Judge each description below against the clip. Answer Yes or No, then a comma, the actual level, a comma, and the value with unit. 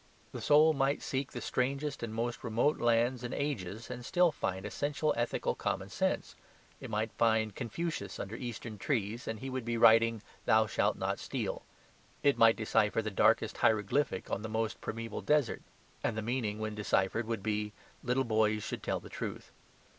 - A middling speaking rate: Yes, average, 175 wpm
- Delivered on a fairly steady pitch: No, average, 3.2 semitones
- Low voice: Yes, low, 115 Hz